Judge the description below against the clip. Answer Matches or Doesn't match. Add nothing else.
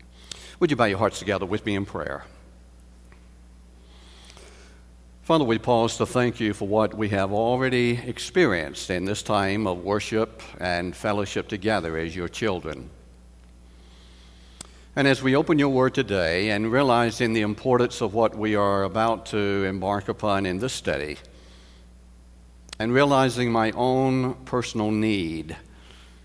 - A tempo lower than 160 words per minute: Matches